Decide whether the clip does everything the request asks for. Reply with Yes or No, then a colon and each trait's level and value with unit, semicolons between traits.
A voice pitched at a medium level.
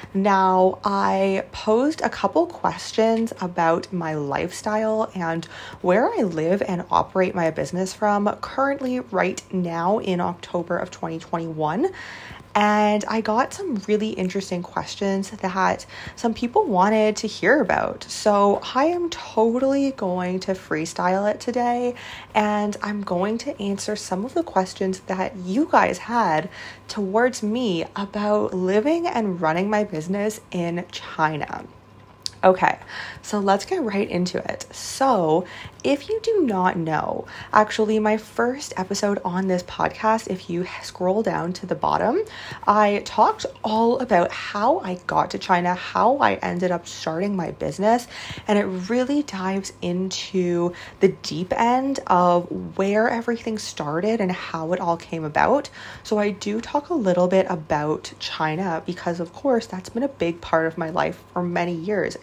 No: high, 195 Hz